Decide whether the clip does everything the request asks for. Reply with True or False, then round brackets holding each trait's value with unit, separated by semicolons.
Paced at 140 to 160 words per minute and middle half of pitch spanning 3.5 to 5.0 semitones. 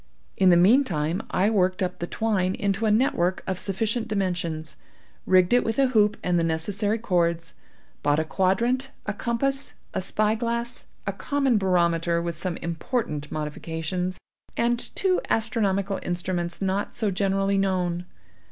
True (150 wpm; 4.3 semitones)